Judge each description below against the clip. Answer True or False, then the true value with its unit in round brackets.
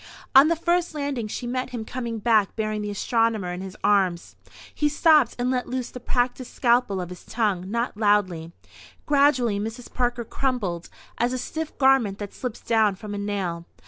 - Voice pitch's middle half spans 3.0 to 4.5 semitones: True (3.9 semitones)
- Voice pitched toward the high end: True (230 Hz)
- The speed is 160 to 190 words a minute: True (180 wpm)